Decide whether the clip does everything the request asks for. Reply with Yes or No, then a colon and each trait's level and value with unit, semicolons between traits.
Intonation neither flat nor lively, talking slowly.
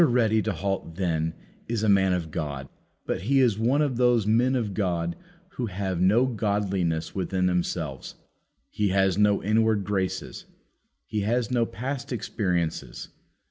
No: average, 4.2 semitones; average, 150 wpm